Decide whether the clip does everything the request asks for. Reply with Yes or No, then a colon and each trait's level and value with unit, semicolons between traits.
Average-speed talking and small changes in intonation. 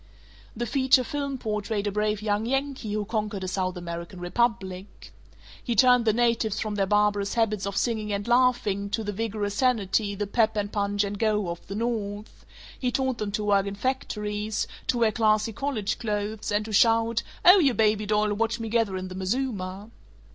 Yes: average, 190 wpm; narrow, 2.3 semitones